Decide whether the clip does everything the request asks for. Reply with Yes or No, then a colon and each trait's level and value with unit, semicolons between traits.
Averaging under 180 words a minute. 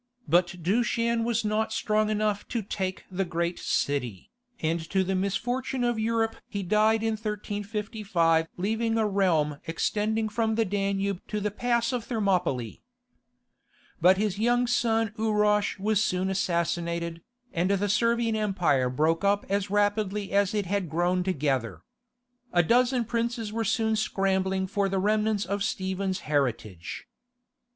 Yes: average, 145 wpm